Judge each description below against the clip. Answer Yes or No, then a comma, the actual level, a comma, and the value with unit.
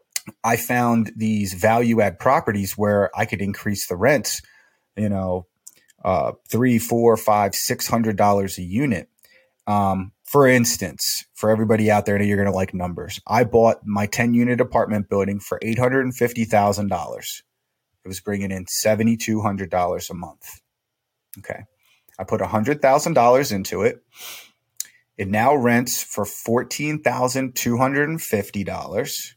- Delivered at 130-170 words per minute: Yes, average, 160 wpm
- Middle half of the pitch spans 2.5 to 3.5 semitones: Yes, average, 3.2 semitones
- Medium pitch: No, low, 110 Hz